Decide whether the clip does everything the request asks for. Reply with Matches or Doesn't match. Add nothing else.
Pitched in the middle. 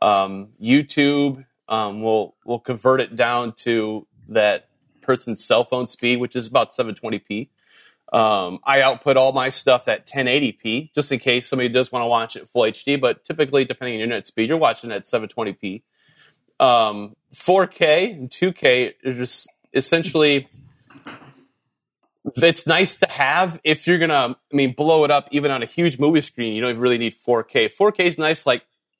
Doesn't match